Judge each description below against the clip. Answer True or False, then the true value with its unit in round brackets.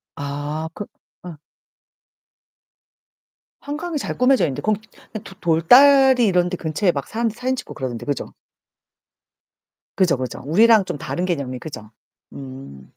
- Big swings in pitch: True (8.4 semitones)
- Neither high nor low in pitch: True (175 Hz)